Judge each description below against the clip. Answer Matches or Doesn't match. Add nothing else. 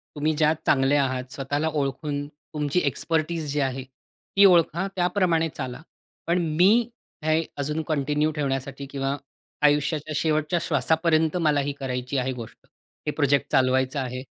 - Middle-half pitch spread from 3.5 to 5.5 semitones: Doesn't match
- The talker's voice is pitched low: Doesn't match